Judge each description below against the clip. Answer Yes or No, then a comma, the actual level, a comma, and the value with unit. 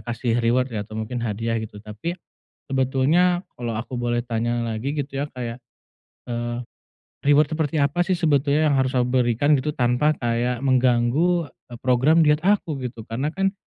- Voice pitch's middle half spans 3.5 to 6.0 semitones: Yes, average, 4.0 semitones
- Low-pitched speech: Yes, low, 130 Hz